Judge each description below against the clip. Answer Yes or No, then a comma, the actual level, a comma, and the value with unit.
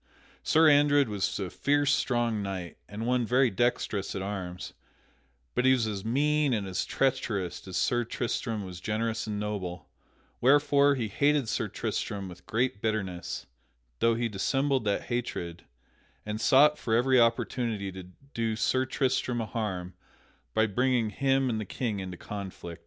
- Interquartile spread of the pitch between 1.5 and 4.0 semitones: No, average, 4.6 semitones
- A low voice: Yes, low, 115 Hz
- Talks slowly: No, average, 155 wpm